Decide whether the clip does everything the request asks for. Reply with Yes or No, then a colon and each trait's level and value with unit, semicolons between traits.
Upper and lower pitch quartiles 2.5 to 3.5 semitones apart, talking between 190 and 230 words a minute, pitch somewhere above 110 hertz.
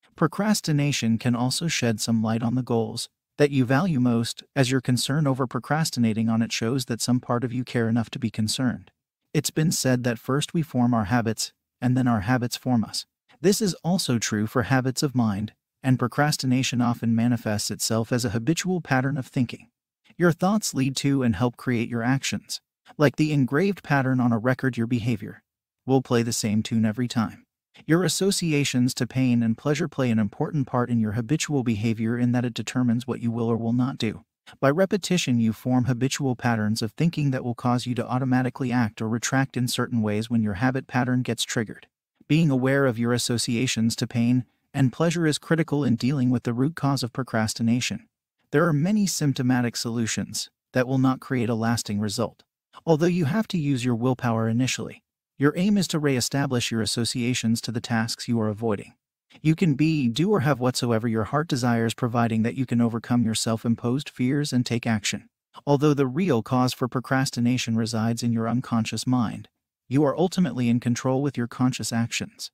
Yes: average, 2.9 semitones; average, 195 wpm; low, 125 Hz